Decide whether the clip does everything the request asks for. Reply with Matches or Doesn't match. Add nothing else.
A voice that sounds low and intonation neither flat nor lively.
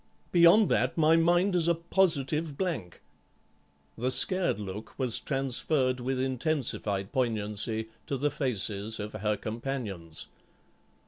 Doesn't match